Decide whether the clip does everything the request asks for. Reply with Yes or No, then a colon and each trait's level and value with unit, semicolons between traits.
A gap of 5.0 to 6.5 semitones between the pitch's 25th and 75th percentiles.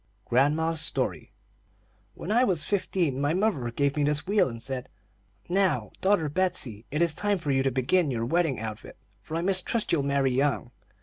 Yes: wide, 5.5 semitones